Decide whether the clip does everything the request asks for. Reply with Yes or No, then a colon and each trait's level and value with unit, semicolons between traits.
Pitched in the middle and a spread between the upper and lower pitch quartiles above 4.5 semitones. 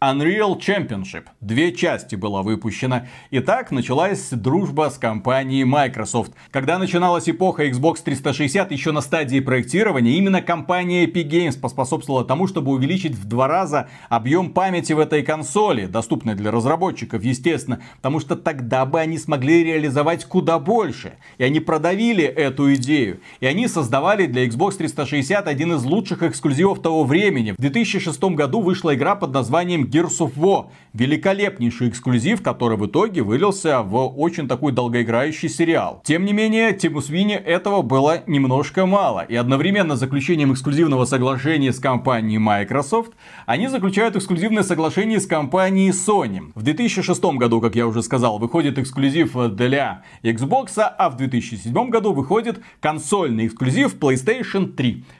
Yes: medium, 155 Hz; wide, 5.5 semitones